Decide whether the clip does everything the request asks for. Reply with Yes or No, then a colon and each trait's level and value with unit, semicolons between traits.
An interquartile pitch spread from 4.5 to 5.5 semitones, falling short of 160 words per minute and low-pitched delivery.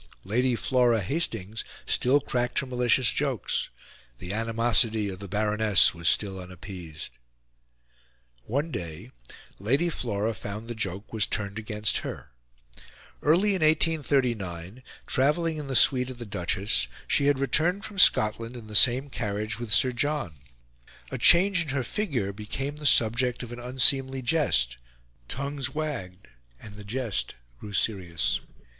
Yes: average, 5.0 semitones; average, 140 wpm; low, 120 Hz